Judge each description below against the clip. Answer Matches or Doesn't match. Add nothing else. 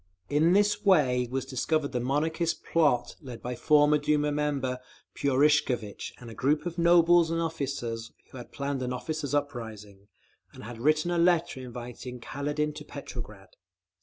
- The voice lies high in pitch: Doesn't match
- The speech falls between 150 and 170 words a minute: Matches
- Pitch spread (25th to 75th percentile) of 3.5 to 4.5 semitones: Matches